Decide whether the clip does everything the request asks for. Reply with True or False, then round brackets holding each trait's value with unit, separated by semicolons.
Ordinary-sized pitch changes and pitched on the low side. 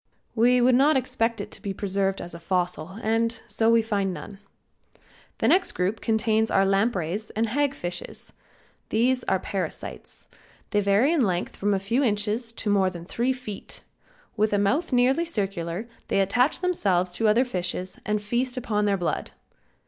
False (3.9 semitones; 210 Hz)